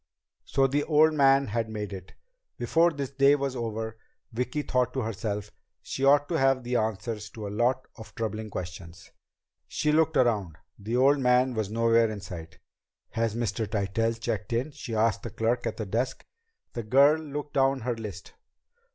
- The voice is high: No, low, 115 Hz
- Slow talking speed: No, average, 175 wpm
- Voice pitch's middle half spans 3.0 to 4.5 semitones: Yes, average, 3.9 semitones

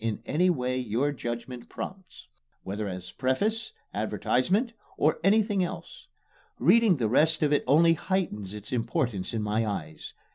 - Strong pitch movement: Yes, wide, 8.5 semitones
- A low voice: Yes, low, 130 Hz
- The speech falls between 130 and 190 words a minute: Yes, average, 145 wpm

